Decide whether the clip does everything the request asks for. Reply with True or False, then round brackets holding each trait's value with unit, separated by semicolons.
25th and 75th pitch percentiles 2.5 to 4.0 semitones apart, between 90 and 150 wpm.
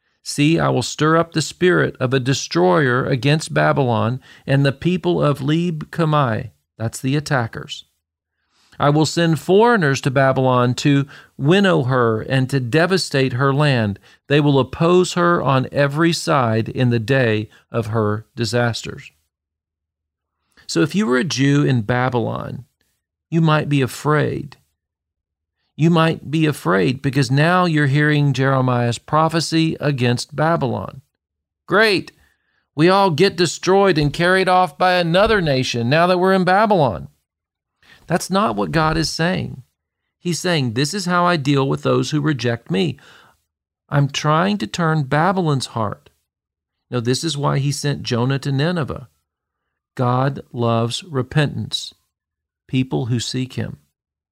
False (5.4 semitones; 140 wpm)